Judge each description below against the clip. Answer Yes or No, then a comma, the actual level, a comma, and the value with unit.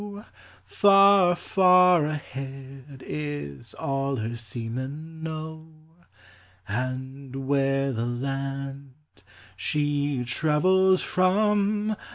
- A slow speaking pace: Yes, slow, 75 wpm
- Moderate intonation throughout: Yes, average, 4.6 semitones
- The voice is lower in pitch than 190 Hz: Yes, medium, 140 Hz